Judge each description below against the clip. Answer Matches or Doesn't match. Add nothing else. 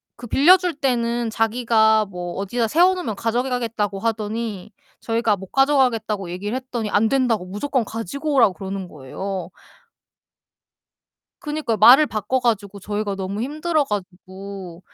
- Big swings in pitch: Doesn't match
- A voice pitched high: Matches